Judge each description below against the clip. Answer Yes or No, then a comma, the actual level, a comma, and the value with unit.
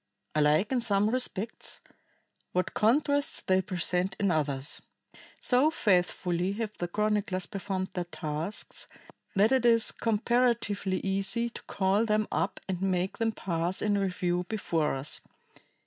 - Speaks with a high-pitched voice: Yes, high, 195 Hz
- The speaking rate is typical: No, slow, 130 wpm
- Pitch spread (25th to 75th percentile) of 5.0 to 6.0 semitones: No, average, 3.5 semitones